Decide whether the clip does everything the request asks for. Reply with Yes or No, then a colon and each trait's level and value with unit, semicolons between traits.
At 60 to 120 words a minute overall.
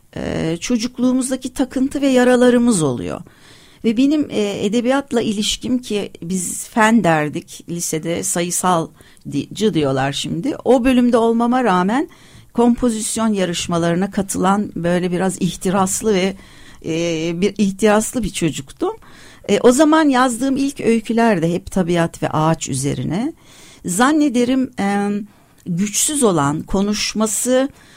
Yes: average, 115 wpm